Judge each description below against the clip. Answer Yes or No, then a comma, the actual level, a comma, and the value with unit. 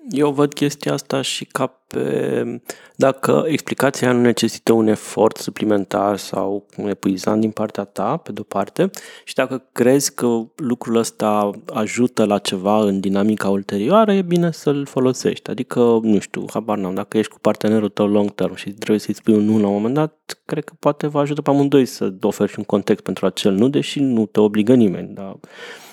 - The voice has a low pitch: Yes, low, 110 Hz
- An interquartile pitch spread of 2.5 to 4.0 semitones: No, average, 4.5 semitones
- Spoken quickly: Yes, fast, 190 wpm